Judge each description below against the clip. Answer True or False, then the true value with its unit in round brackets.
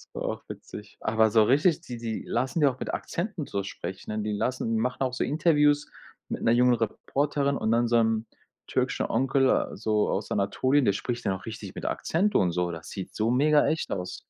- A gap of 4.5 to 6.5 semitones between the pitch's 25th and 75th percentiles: True (4.9 semitones)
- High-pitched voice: False (120 Hz)